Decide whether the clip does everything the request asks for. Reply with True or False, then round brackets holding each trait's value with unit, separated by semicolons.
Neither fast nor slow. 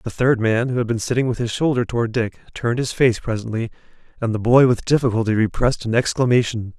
False (210 wpm)